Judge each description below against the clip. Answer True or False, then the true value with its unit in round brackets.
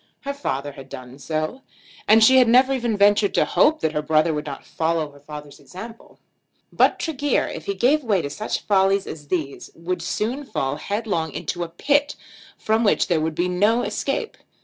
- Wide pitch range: True (7.3 semitones)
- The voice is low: False (190 Hz)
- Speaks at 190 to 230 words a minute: True (195 wpm)